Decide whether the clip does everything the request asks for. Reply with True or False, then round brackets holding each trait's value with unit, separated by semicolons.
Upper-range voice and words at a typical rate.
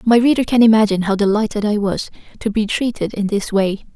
False (210 Hz; 215 wpm)